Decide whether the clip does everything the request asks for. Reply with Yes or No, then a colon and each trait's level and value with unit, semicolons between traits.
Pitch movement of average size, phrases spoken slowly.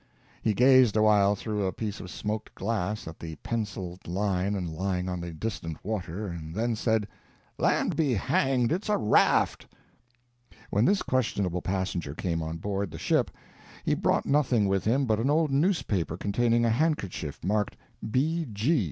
No: average, 4.8 semitones; average, 160 wpm